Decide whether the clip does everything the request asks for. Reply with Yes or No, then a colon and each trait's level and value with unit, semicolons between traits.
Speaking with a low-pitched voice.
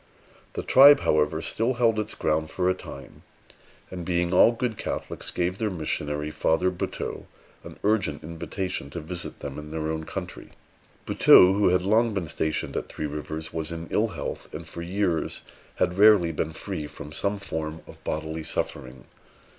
Yes: very low, 85 Hz